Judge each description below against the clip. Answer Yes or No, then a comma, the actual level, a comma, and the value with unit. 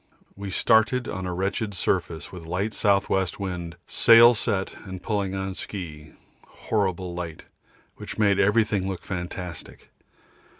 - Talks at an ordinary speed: No, slow, 130 wpm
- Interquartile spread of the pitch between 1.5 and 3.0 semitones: Yes, narrow, 2.6 semitones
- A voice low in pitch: Yes, very low, 95 Hz